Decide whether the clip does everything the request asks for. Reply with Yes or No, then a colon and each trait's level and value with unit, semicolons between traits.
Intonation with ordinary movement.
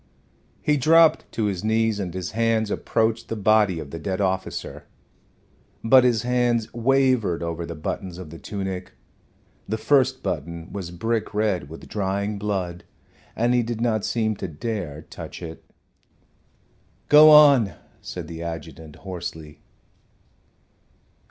Yes: average, 5.0 semitones